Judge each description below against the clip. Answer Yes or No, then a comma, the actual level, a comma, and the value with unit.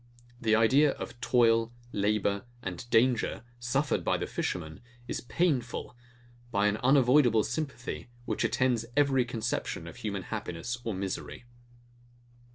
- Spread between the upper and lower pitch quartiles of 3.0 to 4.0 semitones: Yes, average, 3.4 semitones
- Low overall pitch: Yes, low, 120 Hz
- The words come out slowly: Yes, slow, 125 wpm